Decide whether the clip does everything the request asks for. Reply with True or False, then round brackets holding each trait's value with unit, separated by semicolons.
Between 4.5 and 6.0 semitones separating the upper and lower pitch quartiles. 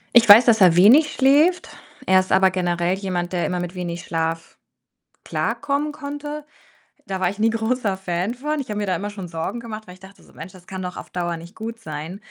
True (4.8 semitones)